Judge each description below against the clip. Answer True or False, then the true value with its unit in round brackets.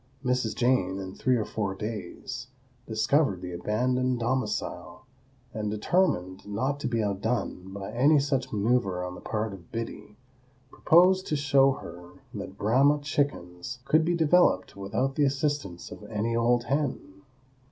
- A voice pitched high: False (115 Hz)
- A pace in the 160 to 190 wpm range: False (145 wpm)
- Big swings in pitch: True (5.7 semitones)